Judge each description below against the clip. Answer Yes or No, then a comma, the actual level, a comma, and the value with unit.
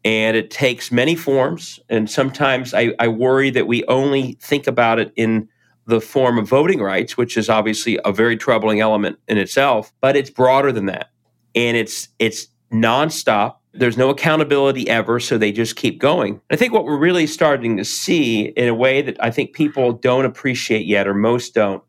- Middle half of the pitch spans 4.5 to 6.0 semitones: No, average, 3.2 semitones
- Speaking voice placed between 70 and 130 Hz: Yes, low, 120 Hz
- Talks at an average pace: Yes, average, 190 wpm